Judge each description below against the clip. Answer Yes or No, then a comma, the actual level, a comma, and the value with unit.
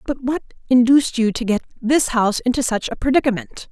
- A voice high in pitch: Yes, high, 245 Hz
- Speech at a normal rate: Yes, average, 195 wpm